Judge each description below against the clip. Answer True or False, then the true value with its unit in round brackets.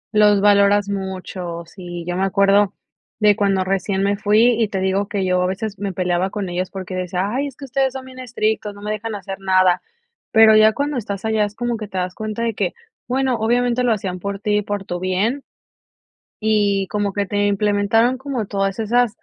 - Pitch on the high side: True (205 Hz)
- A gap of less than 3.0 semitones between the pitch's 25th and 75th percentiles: True (2.5 semitones)